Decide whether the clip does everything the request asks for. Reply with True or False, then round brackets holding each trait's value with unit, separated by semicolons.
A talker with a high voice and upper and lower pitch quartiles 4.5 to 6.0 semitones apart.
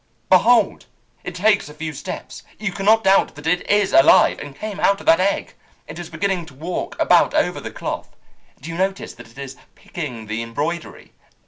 False (170 Hz; 5.3 semitones)